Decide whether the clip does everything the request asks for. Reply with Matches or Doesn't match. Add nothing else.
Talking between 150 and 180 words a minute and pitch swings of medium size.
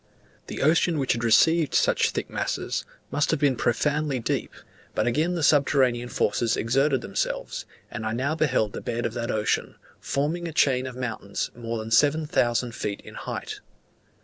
Matches